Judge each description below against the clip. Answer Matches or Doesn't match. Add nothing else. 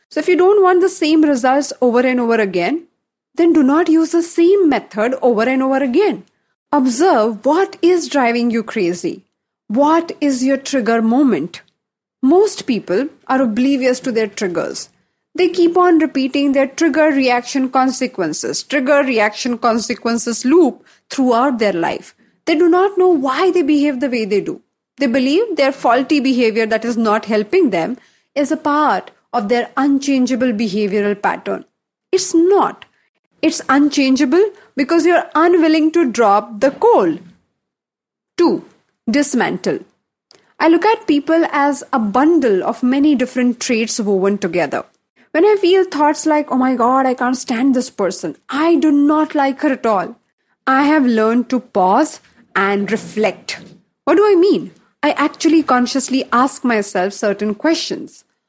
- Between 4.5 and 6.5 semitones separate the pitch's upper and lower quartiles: Matches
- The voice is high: Matches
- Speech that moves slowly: Doesn't match